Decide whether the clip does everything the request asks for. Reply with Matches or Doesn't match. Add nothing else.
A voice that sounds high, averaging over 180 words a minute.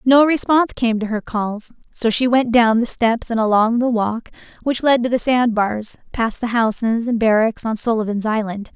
Matches